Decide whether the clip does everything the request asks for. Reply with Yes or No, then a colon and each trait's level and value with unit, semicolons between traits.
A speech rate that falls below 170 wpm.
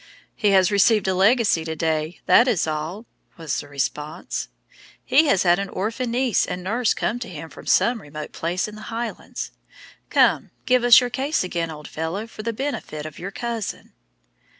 No: average, 185 wpm